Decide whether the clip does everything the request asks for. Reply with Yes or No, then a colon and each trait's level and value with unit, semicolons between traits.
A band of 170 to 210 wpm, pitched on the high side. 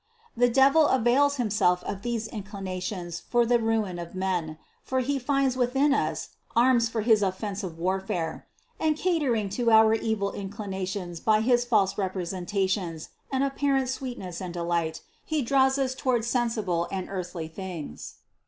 No: average, 150 wpm; high, 215 Hz